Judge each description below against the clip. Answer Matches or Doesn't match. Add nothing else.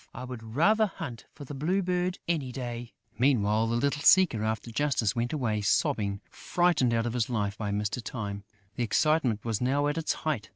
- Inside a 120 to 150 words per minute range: Doesn't match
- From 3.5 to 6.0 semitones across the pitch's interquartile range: Matches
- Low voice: Matches